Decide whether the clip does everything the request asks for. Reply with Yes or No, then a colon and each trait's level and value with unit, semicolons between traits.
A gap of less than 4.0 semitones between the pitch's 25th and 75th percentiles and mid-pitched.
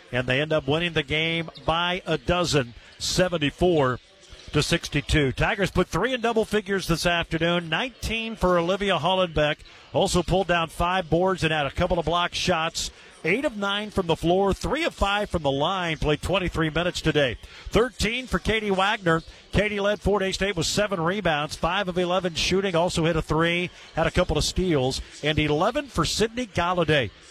Yes: average, 3.4 semitones; medium, 175 Hz